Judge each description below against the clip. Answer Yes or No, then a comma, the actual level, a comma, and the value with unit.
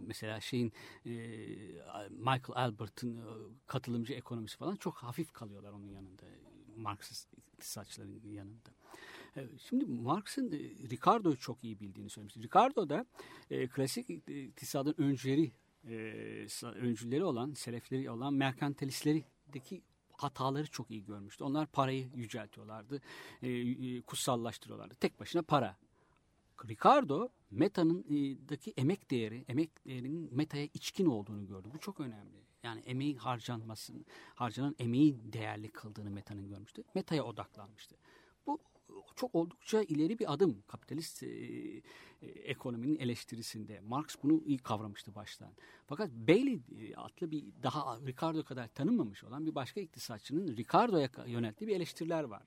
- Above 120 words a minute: No, average, 115 wpm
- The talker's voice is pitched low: Yes, low, 125 Hz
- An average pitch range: Yes, average, 5.0 semitones